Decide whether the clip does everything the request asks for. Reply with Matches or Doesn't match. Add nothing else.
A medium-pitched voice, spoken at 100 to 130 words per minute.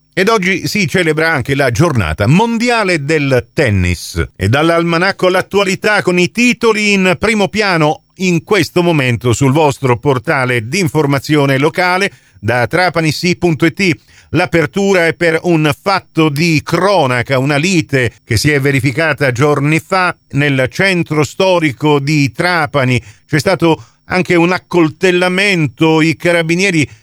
Matches